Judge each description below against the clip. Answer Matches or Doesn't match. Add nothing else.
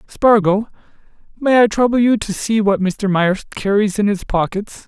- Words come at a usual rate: Matches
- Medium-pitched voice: Doesn't match